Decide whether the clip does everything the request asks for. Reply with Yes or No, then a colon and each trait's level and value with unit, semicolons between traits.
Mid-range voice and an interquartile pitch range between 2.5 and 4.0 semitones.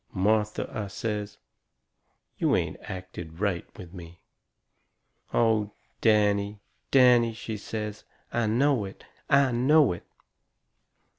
No: low, 105 Hz; average, 2.8 semitones